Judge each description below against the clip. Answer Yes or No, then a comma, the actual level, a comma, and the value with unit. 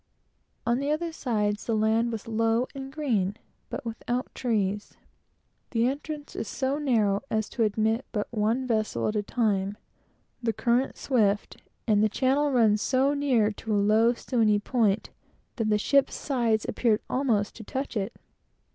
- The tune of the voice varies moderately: Yes, average, 3.5 semitones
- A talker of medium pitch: No, high, 225 Hz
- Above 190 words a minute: No, average, 160 wpm